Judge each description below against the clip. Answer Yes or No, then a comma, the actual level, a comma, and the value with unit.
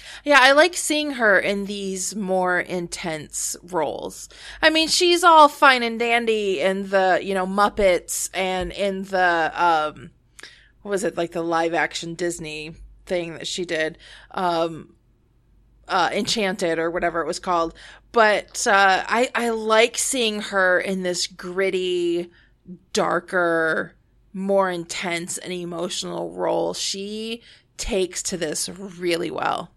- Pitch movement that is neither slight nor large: Yes, average, 3.3 semitones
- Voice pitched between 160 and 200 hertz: Yes, medium, 185 Hz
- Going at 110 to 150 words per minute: Yes, slow, 135 wpm